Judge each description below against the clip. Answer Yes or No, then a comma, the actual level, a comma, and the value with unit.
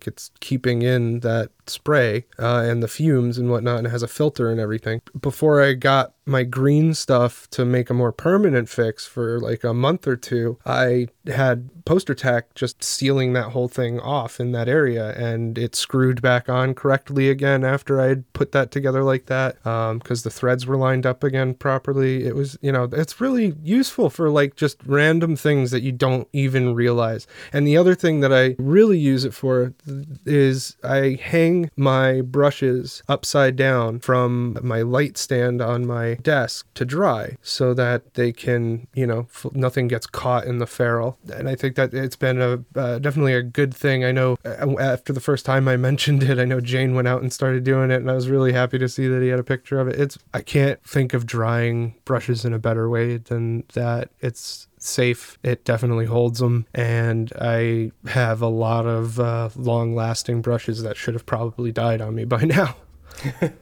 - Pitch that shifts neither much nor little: No, narrow, 2.3 semitones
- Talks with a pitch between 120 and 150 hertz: Yes, low, 125 Hz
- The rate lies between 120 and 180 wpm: No, average, 200 wpm